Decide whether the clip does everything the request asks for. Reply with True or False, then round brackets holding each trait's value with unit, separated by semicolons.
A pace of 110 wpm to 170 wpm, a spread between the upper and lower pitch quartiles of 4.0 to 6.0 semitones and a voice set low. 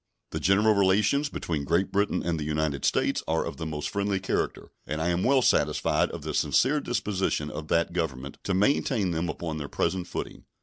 False (200 wpm; 4.5 semitones; 90 Hz)